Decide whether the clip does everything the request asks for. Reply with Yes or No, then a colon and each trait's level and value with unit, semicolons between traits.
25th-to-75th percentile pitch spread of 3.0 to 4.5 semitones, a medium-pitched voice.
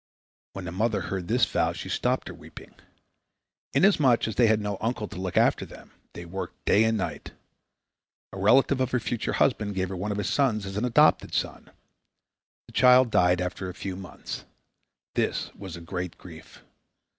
No: average, 4.0 semitones; low, 100 Hz